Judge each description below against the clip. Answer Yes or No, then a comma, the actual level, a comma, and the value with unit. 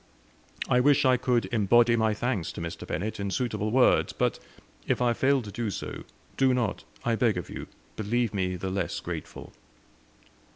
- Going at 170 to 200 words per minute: Yes, average, 175 wpm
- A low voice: Yes, low, 115 Hz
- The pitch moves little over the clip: No, average, 3.7 semitones